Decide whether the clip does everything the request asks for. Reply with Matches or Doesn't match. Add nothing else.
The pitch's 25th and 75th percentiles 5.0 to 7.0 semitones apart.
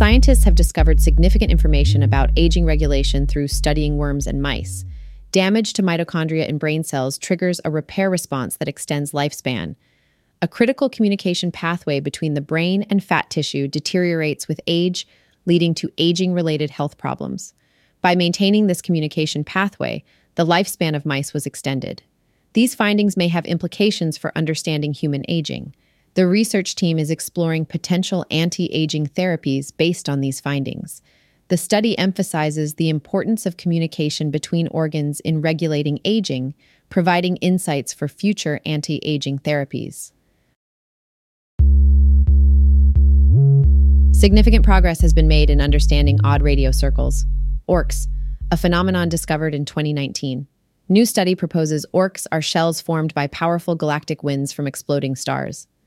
Doesn't match